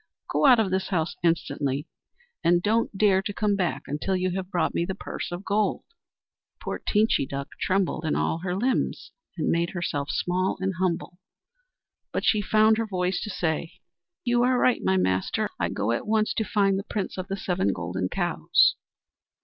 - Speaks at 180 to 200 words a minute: Yes, average, 185 wpm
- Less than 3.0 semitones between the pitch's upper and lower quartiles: No, average, 3.8 semitones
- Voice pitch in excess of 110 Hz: Yes, medium, 185 Hz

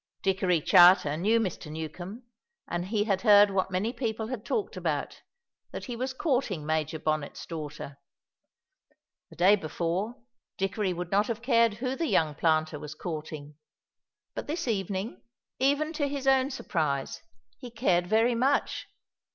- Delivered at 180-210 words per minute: No, average, 150 wpm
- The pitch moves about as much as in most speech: No, wide, 6.6 semitones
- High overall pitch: Yes, high, 195 Hz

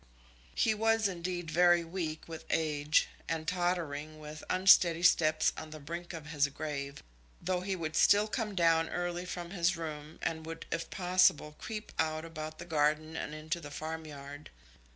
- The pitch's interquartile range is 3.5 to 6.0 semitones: No, narrow, 2.4 semitones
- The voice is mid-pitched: Yes, medium, 165 Hz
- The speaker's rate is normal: Yes, average, 165 wpm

